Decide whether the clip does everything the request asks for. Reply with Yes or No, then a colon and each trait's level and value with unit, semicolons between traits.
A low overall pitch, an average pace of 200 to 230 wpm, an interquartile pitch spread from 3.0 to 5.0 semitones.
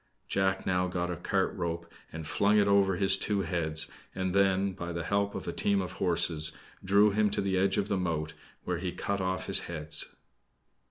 No: very low, 95 Hz; fast, 205 wpm; narrow, 2.5 semitones